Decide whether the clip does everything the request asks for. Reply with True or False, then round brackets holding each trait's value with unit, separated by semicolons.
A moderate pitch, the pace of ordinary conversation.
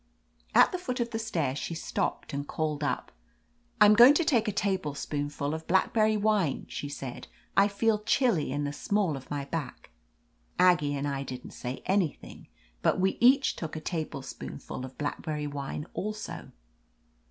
True (160 Hz; 165 wpm)